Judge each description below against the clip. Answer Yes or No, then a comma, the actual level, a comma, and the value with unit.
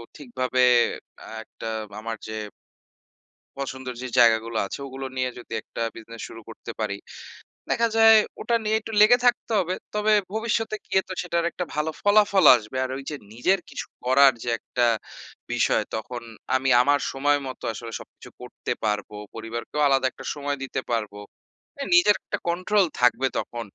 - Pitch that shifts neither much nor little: No, wide, 8.1 semitones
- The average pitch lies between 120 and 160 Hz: Yes, low, 135 Hz